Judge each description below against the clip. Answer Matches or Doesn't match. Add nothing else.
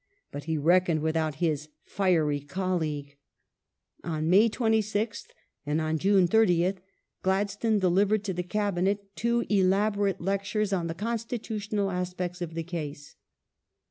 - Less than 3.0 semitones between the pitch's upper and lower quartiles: Doesn't match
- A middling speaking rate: Doesn't match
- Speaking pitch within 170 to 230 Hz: Matches